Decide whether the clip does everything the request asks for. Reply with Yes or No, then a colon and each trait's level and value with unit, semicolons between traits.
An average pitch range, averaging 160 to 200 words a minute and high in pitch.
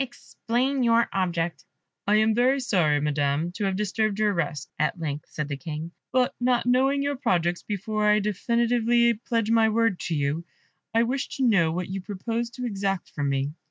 No: wide, 5.9 semitones; average, 185 wpm; high, 210 Hz